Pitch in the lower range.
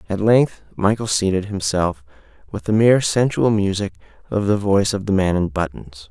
Yes: low, 100 Hz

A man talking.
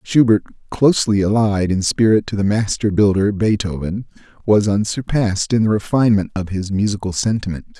Yes: male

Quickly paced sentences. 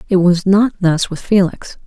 No: average, 195 wpm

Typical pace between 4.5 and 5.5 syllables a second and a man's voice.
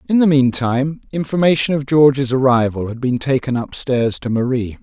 Yes: 5.1 syllables/s; male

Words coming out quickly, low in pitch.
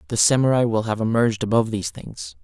No: average, 195 wpm; low, 115 Hz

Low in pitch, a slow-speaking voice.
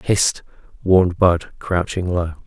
Yes: very low, 90 Hz; slow, 120 wpm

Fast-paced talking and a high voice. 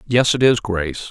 No: fast, 215 wpm; low, 110 Hz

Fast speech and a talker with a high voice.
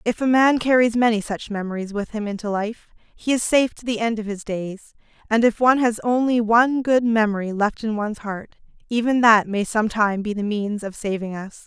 Yes: fast, 215 wpm; high, 220 Hz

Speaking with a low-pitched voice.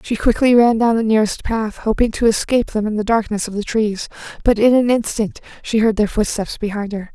No: high, 220 Hz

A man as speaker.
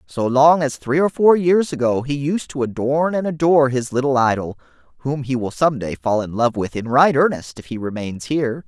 Yes: male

